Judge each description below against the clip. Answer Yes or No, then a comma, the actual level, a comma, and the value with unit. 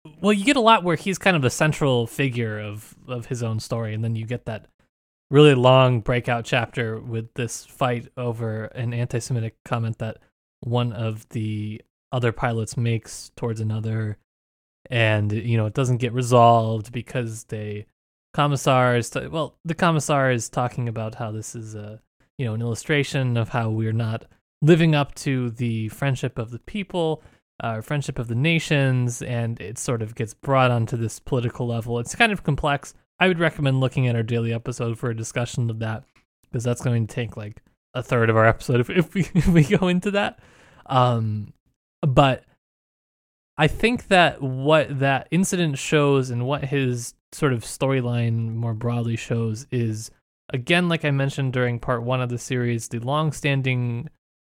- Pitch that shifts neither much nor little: Yes, average, 3.5 semitones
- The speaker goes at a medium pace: Yes, average, 180 wpm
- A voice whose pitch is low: Yes, low, 125 Hz